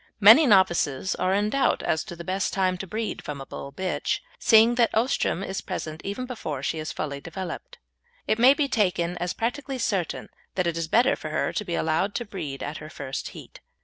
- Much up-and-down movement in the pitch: Yes, wide, 5.7 semitones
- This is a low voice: No, high, 190 Hz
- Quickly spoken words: Yes, fast, 210 wpm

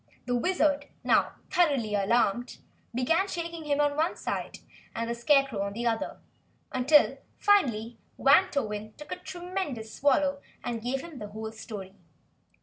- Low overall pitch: No, very high, 265 Hz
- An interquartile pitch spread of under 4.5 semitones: No, wide, 5.4 semitones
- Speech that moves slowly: No, average, 145 wpm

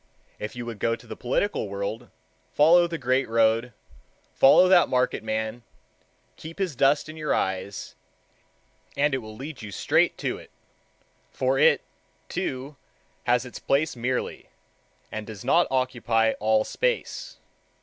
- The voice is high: No, low, 125 Hz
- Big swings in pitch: No, average, 4.8 semitones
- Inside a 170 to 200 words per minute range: No, average, 140 wpm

